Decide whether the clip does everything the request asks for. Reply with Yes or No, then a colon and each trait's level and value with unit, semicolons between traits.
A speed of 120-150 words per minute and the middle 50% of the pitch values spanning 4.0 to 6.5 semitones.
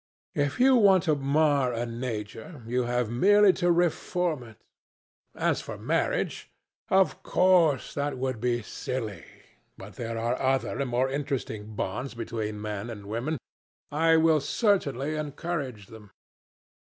Yes: average, 140 wpm; wide, 5.4 semitones